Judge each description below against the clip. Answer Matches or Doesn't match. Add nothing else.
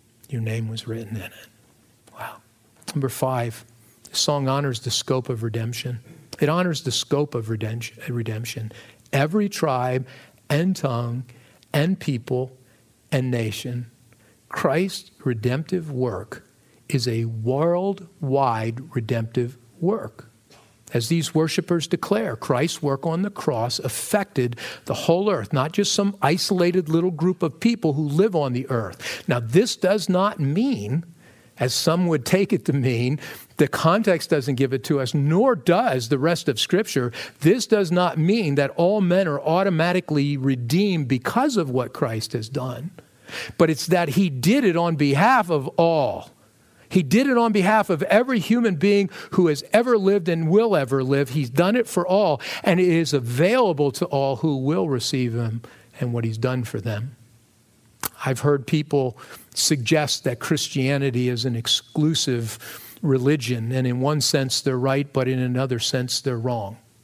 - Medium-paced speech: Matches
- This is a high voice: Doesn't match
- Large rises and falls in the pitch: Matches